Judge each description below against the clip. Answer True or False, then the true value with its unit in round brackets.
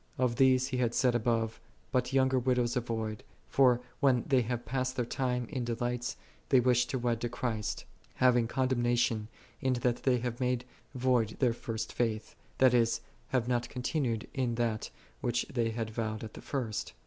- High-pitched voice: False (120 Hz)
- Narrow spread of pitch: True (1.7 semitones)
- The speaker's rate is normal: True (185 wpm)